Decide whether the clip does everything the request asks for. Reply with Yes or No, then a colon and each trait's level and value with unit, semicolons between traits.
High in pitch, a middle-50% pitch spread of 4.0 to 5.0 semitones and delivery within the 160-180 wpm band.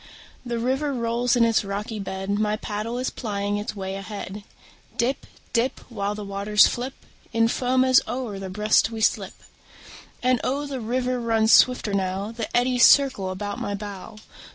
No: high, 220 Hz; average, 3.4 semitones; average, 170 wpm